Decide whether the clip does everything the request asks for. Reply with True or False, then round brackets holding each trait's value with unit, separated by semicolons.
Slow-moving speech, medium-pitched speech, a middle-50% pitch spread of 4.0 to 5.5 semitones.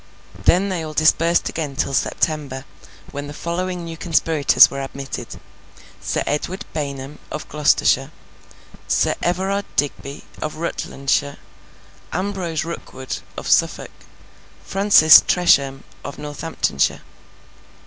False (105 wpm; 155 Hz; 3.5 semitones)